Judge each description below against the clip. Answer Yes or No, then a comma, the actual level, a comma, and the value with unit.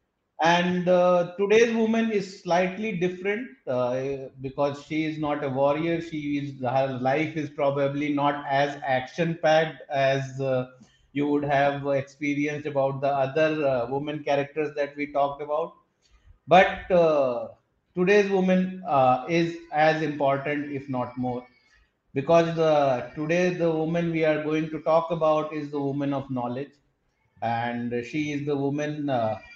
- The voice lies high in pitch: No, medium, 145 Hz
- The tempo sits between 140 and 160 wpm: Yes, average, 150 wpm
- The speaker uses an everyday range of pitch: Yes, average, 3.3 semitones